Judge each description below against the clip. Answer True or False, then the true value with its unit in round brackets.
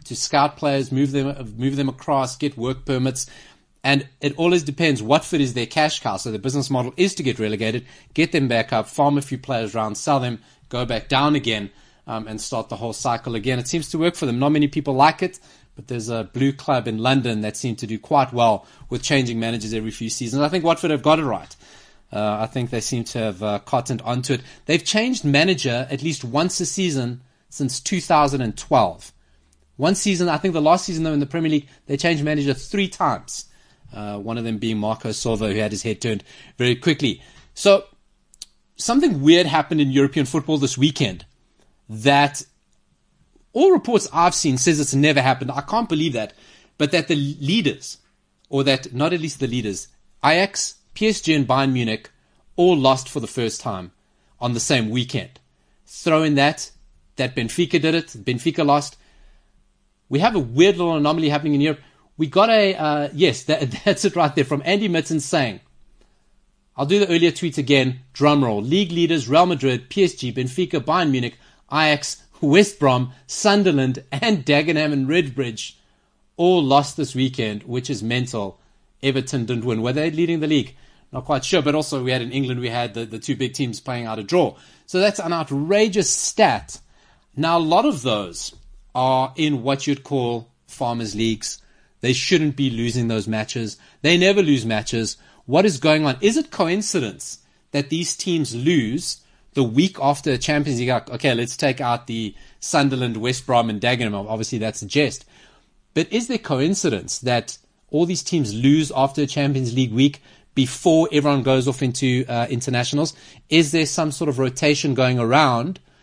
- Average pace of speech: True (190 wpm)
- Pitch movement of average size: True (4.5 semitones)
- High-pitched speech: False (140 Hz)